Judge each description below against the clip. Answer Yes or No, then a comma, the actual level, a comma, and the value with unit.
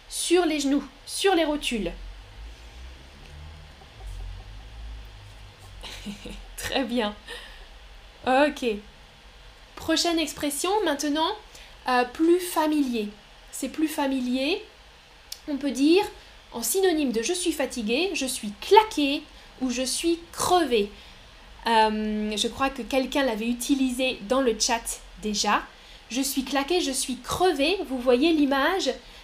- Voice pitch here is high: Yes, very high, 265 Hz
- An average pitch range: No, wide, 6.3 semitones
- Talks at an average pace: No, slow, 110 wpm